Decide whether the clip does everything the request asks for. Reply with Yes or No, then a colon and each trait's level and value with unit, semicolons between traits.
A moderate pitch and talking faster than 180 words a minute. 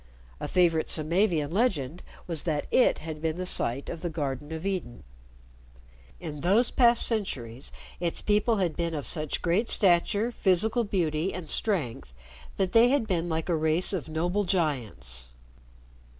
No: medium, 170 Hz; average, 155 wpm